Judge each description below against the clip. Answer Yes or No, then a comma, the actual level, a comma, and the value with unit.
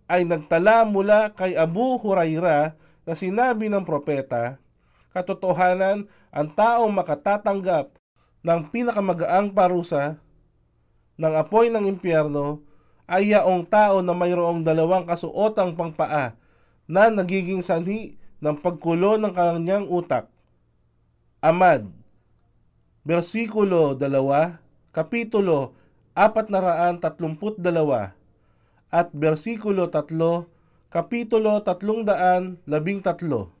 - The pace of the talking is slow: Yes, slow, 90 wpm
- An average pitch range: Yes, average, 4.6 semitones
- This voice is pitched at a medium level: Yes, medium, 175 Hz